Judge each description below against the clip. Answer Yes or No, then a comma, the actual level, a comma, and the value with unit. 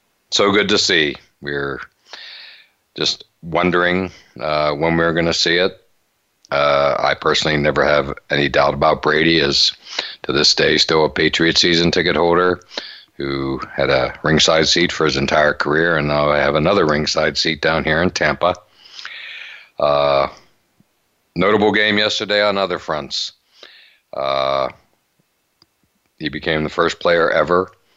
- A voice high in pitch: No, very low, 75 Hz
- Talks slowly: No, average, 145 wpm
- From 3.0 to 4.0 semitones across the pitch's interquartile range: Yes, average, 3.6 semitones